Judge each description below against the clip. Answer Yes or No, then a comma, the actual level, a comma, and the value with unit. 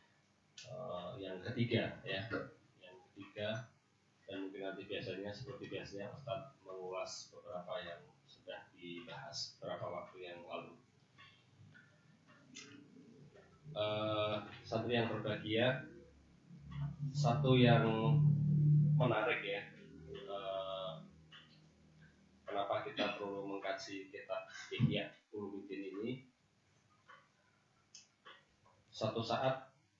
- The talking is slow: Yes, slow, 80 wpm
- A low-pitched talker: Yes, low, 110 Hz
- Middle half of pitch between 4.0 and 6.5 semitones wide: Yes, average, 5.1 semitones